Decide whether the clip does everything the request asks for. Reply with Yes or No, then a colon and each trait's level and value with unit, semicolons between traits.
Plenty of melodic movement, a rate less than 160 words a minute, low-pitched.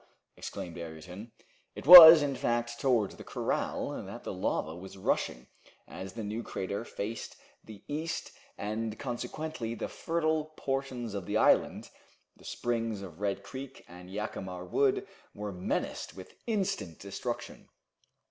Yes: wide, 6.0 semitones; average, 140 wpm; low, 110 Hz